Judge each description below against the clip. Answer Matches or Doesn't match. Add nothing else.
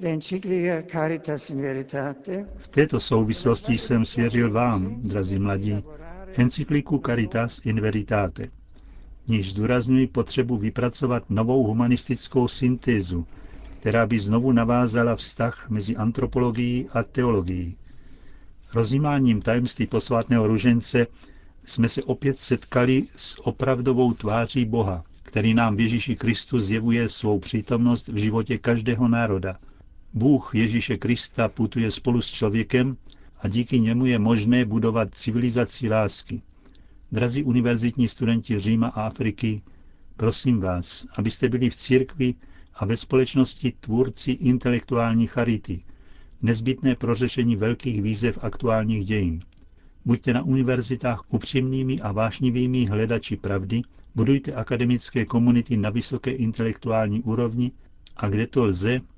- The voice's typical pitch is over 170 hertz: Doesn't match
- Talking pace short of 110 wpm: Doesn't match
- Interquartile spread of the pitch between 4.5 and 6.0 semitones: Doesn't match